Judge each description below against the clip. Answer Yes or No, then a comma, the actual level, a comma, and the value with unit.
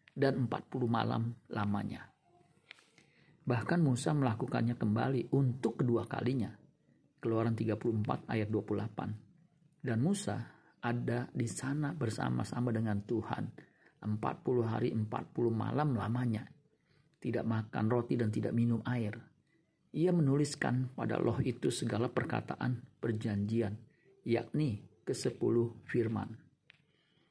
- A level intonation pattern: No, average, 3.4 semitones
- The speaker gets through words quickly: No, average, 100 wpm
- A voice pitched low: Yes, low, 120 Hz